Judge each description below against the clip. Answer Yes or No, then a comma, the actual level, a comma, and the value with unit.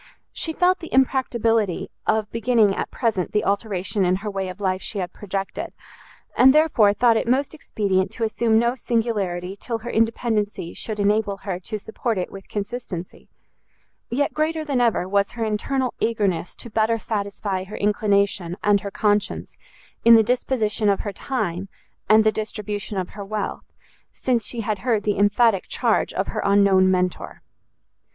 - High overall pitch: Yes, high, 210 Hz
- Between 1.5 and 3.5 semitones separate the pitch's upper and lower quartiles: Yes, average, 2.8 semitones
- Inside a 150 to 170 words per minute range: Yes, average, 165 wpm